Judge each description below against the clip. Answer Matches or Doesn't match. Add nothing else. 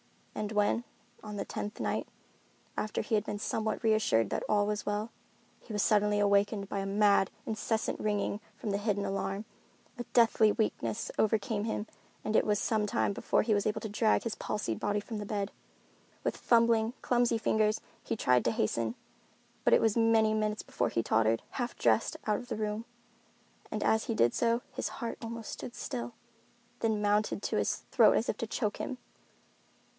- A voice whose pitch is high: Matches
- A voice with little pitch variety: Matches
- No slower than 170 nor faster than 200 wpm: Matches